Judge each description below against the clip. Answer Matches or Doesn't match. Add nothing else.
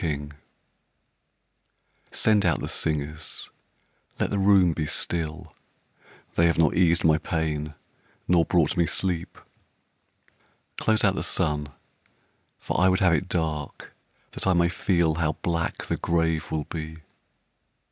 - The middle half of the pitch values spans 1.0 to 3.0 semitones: Matches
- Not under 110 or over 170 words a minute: Matches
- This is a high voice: Doesn't match